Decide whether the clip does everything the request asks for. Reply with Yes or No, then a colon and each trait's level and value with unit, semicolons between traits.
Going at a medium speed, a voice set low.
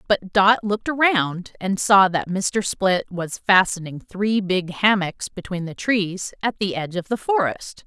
No: average, 175 wpm; high, 195 Hz